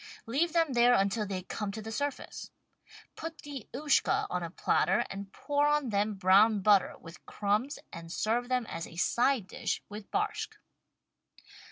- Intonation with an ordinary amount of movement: No, wide, 5.8 semitones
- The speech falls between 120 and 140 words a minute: No, average, 165 wpm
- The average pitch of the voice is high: Yes, high, 220 Hz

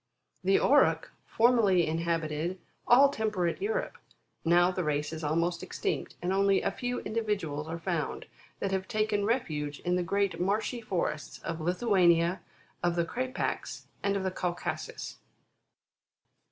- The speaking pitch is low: No, medium, 185 Hz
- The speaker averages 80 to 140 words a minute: Yes, slow, 135 wpm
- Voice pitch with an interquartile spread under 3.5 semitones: No, average, 4.2 semitones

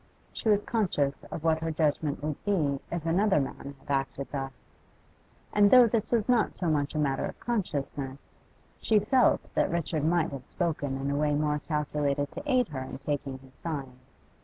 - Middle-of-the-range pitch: Yes, medium, 150 Hz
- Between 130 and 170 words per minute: No, average, 185 wpm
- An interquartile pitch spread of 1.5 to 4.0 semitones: No, average, 4.8 semitones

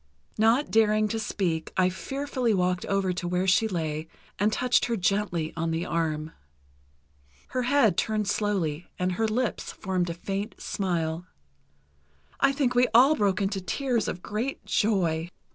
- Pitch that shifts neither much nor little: Yes, average, 4.3 semitones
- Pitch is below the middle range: No, high, 195 Hz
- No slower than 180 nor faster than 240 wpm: No, average, 155 wpm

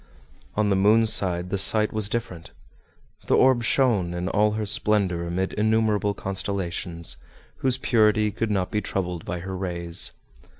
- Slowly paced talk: No, average, 155 wpm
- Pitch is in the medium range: No, low, 100 Hz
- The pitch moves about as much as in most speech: Yes, average, 3.1 semitones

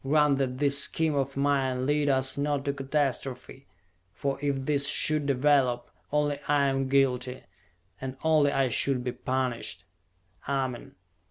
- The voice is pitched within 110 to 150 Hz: Yes, low, 135 Hz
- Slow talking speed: No, average, 145 wpm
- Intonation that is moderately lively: No, narrow, 1.6 semitones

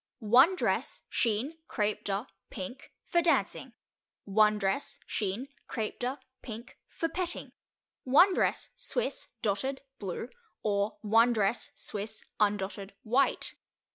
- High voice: Yes, high, 220 Hz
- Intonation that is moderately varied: Yes, average, 4.5 semitones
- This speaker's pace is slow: Yes, slow, 115 wpm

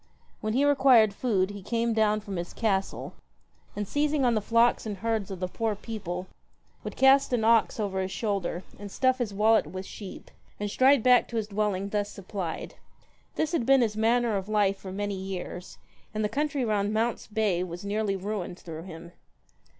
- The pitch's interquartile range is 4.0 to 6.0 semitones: No, average, 3.1 semitones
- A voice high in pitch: Yes, high, 210 Hz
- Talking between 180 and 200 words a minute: Yes, average, 190 wpm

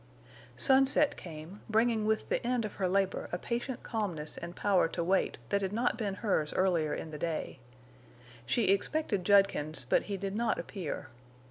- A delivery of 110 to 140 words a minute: No, average, 170 wpm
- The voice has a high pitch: Yes, high, 195 Hz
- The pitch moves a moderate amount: Yes, average, 4.5 semitones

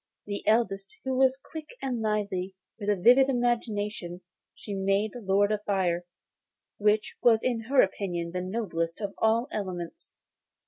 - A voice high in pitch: Yes, high, 210 Hz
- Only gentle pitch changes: No, average, 3.5 semitones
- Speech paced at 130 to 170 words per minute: Yes, average, 150 wpm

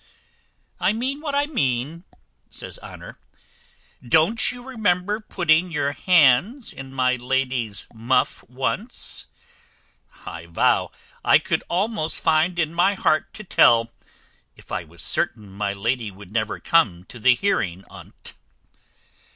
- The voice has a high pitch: No, medium, 140 Hz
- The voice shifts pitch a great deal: Yes, wide, 8.3 semitones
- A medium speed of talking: No, slow, 130 wpm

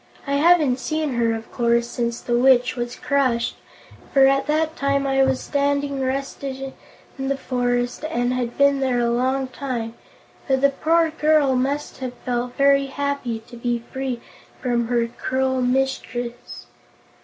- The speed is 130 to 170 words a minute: Yes, average, 155 wpm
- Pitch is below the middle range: No, very high, 265 Hz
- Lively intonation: No, narrow, 2.4 semitones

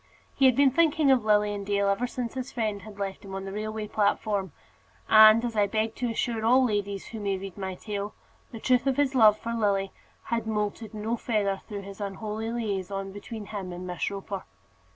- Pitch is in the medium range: No, high, 210 Hz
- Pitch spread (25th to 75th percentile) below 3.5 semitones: Yes, narrow, 2.6 semitones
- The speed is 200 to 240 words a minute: Yes, fast, 205 wpm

